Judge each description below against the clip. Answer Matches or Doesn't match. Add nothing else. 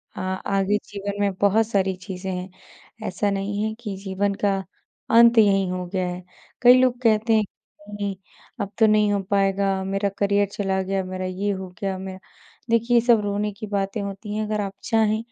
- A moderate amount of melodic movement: Doesn't match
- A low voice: Doesn't match